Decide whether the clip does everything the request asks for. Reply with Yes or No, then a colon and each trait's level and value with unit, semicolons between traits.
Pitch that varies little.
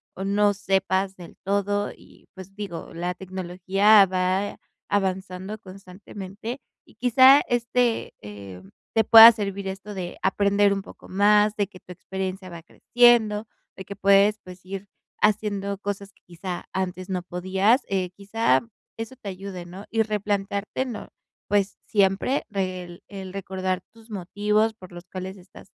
Yes: narrow, 1.9 semitones